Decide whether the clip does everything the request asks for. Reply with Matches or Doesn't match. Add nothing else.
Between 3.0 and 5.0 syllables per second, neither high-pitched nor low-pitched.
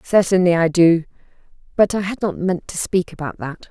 Doesn't match